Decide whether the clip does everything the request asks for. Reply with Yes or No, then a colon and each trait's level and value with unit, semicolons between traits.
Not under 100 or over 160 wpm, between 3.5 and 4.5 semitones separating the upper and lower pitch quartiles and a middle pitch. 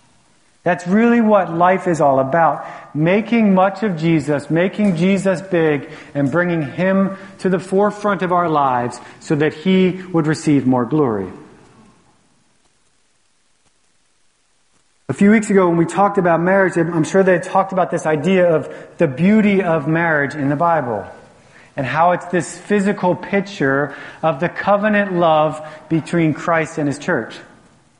Yes: average, 150 wpm; average, 3.8 semitones; medium, 170 Hz